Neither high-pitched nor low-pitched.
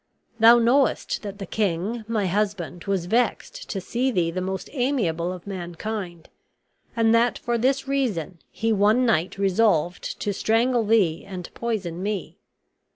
No: high, 205 Hz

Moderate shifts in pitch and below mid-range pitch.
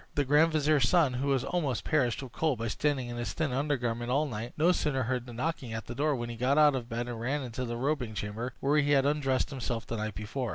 Yes: average, 3.6 semitones; low, 130 Hz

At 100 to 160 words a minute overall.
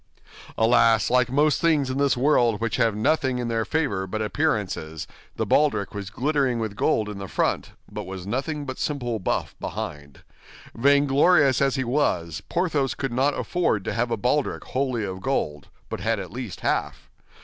No: average, 175 wpm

